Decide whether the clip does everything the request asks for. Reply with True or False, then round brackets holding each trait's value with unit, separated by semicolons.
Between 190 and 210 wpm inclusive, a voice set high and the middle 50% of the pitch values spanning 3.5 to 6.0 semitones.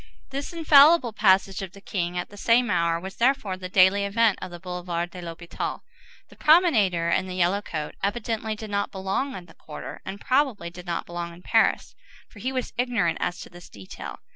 True (200 wpm; 195 Hz; 4.8 semitones)